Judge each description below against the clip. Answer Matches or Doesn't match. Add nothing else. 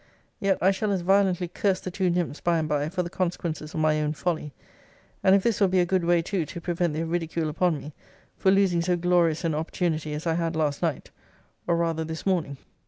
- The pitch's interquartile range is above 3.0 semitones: Doesn't match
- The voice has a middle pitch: Matches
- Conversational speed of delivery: Doesn't match